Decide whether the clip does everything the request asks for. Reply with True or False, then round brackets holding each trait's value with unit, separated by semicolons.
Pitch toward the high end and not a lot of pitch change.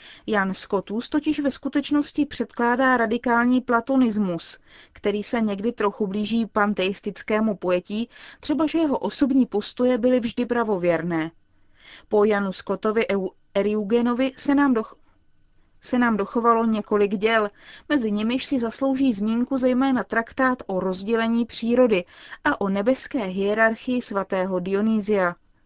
False (230 Hz; 3.7 semitones)